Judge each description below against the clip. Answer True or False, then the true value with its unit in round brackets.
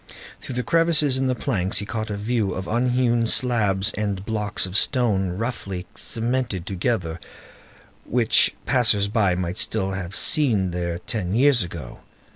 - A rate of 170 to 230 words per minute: False (150 wpm)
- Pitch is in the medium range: False (105 Hz)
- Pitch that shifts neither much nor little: True (4.5 semitones)